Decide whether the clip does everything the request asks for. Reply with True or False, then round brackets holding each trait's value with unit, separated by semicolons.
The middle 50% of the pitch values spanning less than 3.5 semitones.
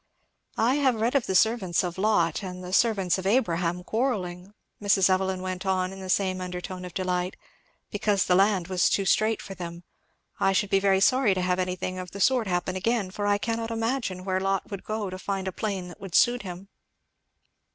True (2.5 semitones)